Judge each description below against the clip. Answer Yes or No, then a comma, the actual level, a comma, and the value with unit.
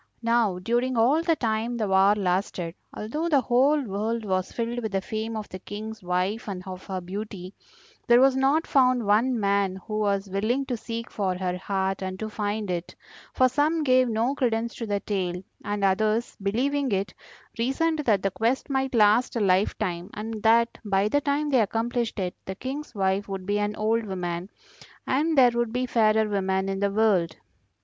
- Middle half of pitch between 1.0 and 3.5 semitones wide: No, average, 3.9 semitones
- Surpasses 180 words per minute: Yes, average, 190 wpm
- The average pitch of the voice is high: Yes, high, 215 Hz